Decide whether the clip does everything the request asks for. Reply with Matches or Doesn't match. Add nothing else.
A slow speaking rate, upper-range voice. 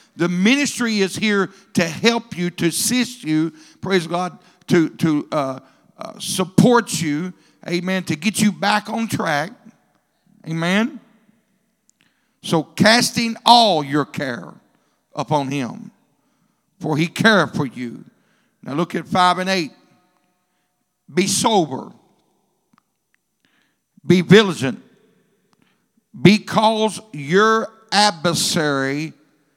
Matches